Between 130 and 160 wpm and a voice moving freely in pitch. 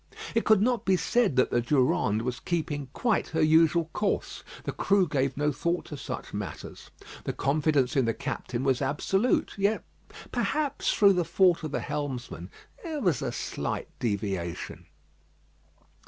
Yes: average, 155 wpm; wide, 6.7 semitones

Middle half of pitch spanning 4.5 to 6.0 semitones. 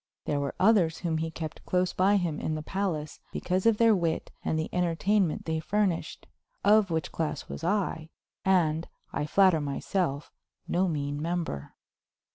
No: average, 3.3 semitones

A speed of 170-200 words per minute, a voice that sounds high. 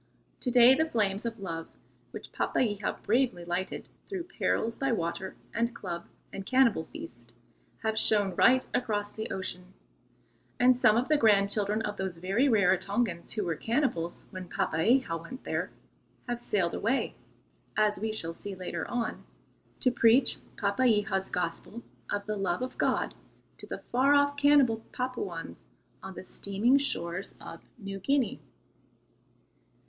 No: average, 145 wpm; high, 215 Hz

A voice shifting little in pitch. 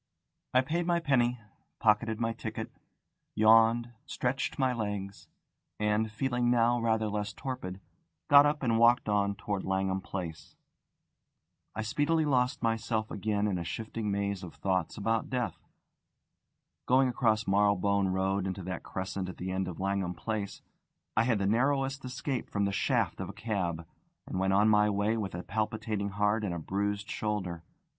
No: average, 3.4 semitones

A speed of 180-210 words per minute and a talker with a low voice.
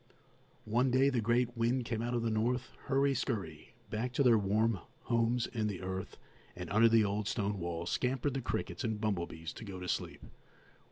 Yes: average, 190 wpm; low, 115 Hz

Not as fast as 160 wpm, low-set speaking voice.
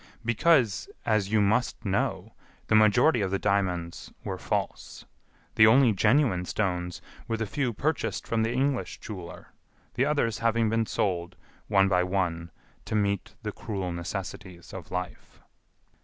Yes: average, 145 wpm; low, 105 Hz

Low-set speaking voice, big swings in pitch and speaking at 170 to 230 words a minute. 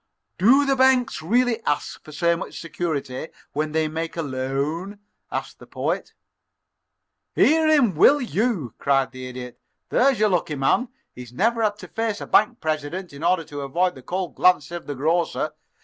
No: medium, 170 Hz; wide, 7.3 semitones; average, 175 wpm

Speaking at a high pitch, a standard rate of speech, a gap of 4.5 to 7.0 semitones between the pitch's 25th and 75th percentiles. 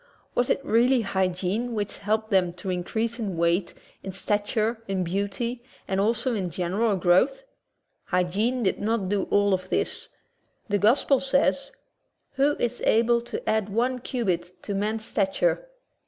No: high, 210 Hz; average, 155 wpm; average, 3.8 semitones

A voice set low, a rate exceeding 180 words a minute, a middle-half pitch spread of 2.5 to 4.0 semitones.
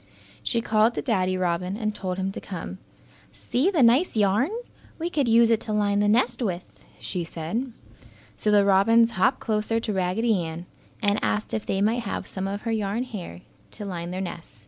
No: high, 210 Hz; average, 195 wpm; average, 3.6 semitones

